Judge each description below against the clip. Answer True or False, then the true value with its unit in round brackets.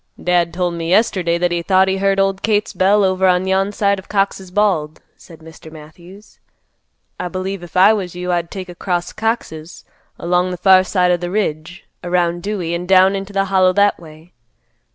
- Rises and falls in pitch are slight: True (2.1 semitones)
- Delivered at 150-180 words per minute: False (195 wpm)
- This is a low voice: False (185 Hz)